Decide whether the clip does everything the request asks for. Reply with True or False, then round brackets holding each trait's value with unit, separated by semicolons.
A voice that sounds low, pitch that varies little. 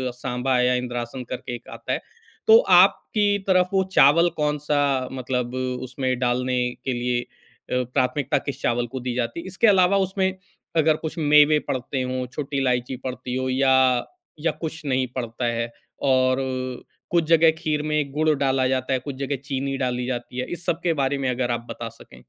False (130 Hz; 3.3 semitones)